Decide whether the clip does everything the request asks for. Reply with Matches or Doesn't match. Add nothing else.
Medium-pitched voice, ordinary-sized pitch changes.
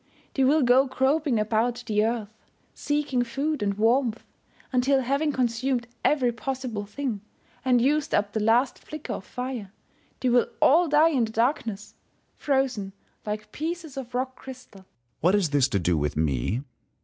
Doesn't match